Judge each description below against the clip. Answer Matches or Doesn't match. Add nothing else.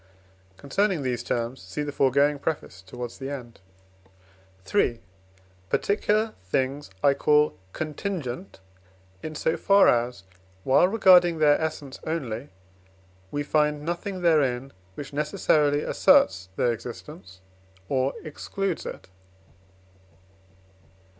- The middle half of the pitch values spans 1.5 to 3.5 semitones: Doesn't match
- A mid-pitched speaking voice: Matches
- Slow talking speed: Matches